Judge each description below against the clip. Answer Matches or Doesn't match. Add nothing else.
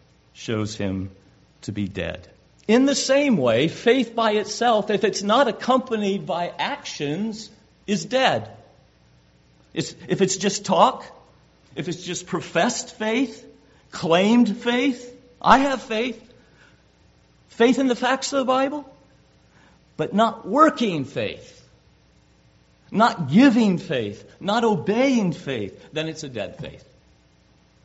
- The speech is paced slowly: Matches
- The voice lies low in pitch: Doesn't match